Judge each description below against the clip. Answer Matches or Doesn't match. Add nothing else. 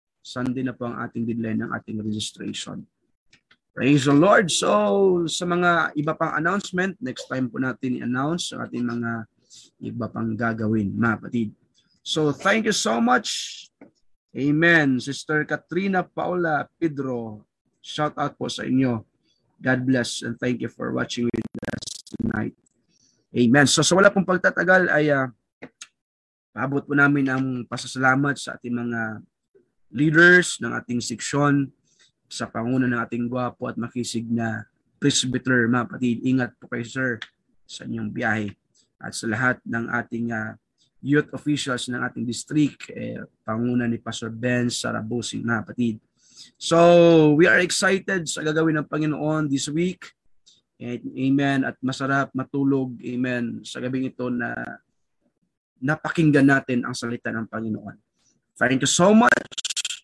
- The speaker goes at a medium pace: Matches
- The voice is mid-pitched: Doesn't match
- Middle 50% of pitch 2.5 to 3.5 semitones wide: Doesn't match